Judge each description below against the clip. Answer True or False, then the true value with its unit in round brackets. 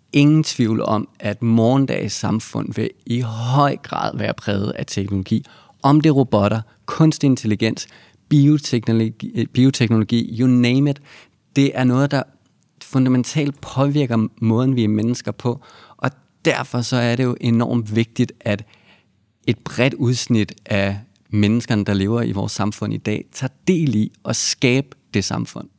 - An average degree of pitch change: True (3.6 semitones)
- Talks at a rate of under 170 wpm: True (150 wpm)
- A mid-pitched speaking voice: False (120 Hz)